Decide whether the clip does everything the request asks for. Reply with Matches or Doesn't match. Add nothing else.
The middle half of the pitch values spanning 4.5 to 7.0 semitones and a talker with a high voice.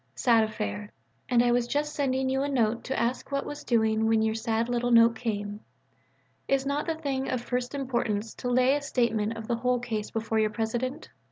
Doesn't match